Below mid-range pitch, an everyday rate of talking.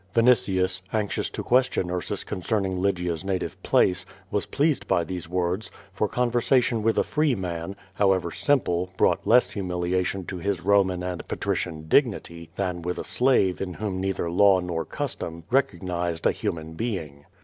Yes: very low, 95 Hz; average, 155 wpm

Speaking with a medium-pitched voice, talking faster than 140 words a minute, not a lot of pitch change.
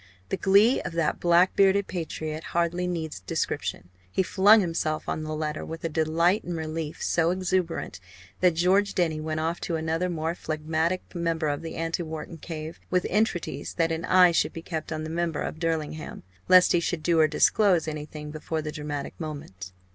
Yes: medium, 165 Hz; average, 185 wpm; narrow, 2.1 semitones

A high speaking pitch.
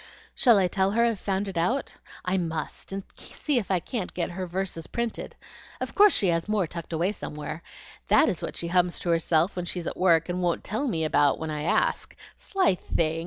No: medium, 180 Hz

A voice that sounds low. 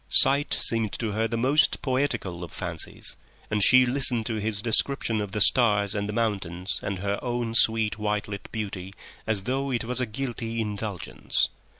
Yes: low, 110 Hz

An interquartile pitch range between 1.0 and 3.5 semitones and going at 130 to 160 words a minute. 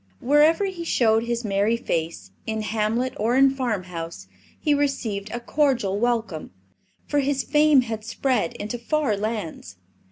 No: average, 4.6 semitones; average, 140 wpm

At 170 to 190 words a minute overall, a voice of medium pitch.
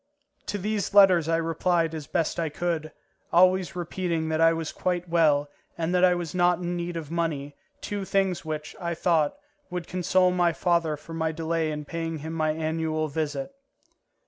Yes: average, 180 wpm; medium, 165 Hz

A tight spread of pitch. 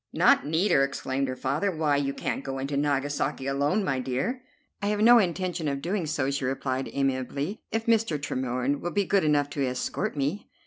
No: average, 5.1 semitones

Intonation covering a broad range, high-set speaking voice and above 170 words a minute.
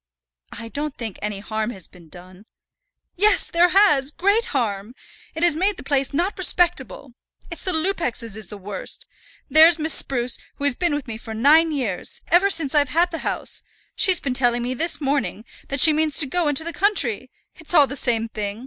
Yes: wide, 6.6 semitones; very high, 280 Hz; average, 200 wpm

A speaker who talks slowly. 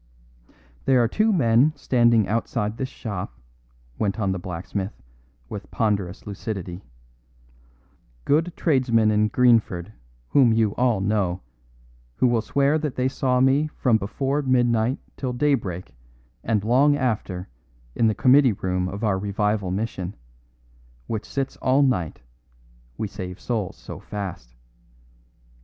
Yes: slow, 130 wpm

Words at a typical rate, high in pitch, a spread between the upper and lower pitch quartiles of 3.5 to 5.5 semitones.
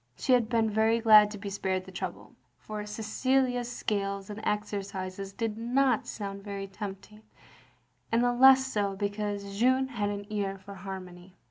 No: average, 160 wpm; high, 210 Hz; narrow, 2.6 semitones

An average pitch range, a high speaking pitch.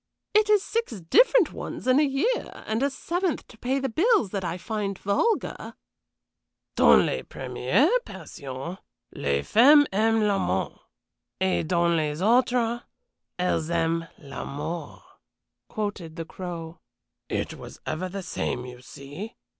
No: wide, 7.6 semitones; high, 195 Hz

